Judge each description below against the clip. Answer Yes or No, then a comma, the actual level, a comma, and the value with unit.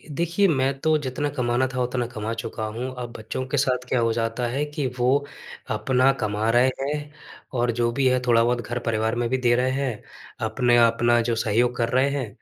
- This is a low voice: Yes, low, 125 Hz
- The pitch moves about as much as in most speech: No, narrow, 2.3 semitones